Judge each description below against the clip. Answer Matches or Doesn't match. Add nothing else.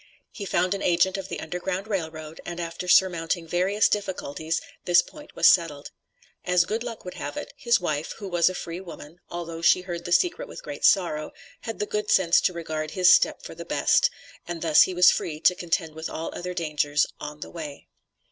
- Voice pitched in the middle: Matches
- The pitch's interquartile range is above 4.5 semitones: Doesn't match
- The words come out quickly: Matches